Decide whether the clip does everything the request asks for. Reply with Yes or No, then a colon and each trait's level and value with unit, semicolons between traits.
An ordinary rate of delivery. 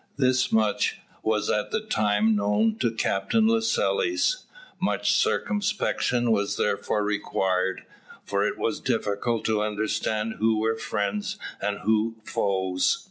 No: slow, 125 wpm